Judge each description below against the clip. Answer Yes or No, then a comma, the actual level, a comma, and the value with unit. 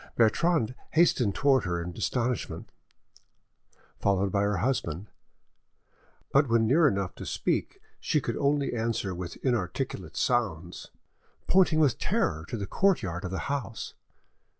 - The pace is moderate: No, slow, 130 wpm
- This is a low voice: Yes, low, 115 Hz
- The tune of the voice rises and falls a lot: Yes, wide, 6.4 semitones